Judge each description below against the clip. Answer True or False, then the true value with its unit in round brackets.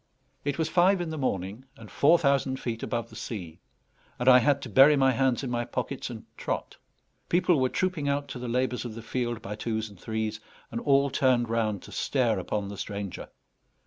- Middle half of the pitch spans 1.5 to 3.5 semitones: False (4.0 semitones)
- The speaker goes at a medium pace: False (210 wpm)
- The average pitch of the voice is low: True (125 Hz)